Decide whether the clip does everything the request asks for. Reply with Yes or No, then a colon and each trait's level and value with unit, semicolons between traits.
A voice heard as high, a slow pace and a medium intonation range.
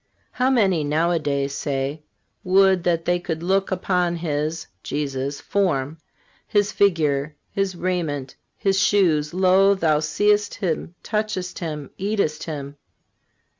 No: medium, 170 Hz; slow, 120 wpm; average, 4.3 semitones